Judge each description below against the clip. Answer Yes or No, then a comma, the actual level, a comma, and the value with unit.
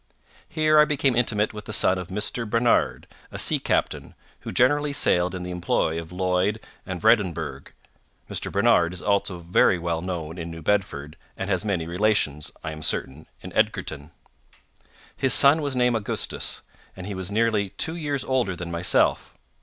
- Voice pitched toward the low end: Yes, very low, 95 Hz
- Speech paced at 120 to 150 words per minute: No, average, 170 wpm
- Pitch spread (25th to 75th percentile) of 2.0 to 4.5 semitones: No, average, 5.3 semitones